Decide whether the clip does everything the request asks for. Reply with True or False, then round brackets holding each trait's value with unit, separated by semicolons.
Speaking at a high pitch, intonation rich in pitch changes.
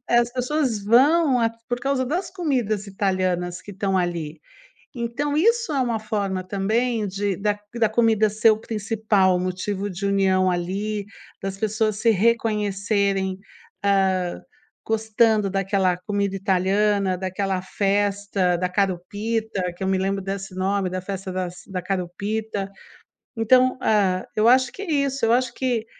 False (200 Hz; 3.0 semitones)